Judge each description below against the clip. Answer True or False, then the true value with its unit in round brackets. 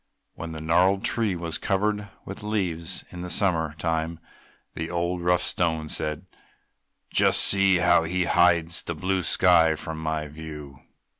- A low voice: True (85 Hz)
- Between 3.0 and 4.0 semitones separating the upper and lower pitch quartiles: False (2.4 semitones)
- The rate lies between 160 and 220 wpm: False (150 wpm)